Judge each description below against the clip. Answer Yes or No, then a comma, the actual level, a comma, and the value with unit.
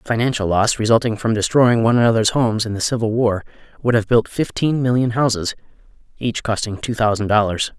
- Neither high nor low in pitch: No, low, 115 Hz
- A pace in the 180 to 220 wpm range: Yes, average, 185 wpm